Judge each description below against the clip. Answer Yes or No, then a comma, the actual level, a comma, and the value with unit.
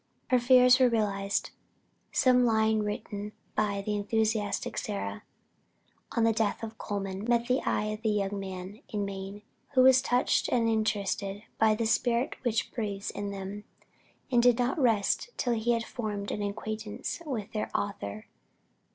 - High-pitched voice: Yes, high, 215 Hz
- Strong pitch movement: No, average, 2.7 semitones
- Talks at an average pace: Yes, average, 160 wpm